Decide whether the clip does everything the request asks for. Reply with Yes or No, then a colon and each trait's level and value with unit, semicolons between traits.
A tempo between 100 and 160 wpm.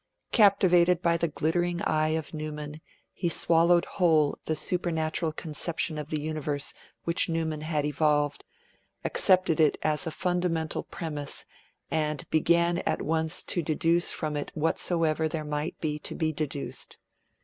Yes: average, 140 wpm